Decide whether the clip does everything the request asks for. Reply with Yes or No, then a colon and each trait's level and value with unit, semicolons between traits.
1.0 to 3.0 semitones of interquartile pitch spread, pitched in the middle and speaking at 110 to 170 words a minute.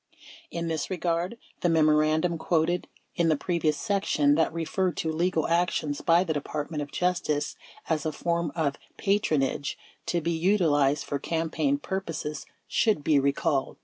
Yes: narrow, 2.6 semitones; medium, 165 Hz; average, 150 wpm